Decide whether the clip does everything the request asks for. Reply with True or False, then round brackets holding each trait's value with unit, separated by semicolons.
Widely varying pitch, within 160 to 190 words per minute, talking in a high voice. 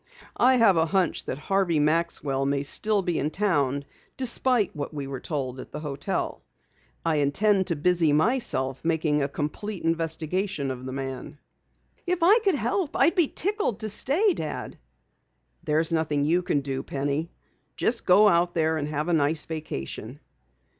False (5.9 semitones; 165 wpm; 160 Hz)